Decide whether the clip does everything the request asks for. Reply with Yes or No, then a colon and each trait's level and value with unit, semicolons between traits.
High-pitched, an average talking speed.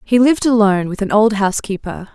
Yes: high, 210 Hz; average, 195 wpm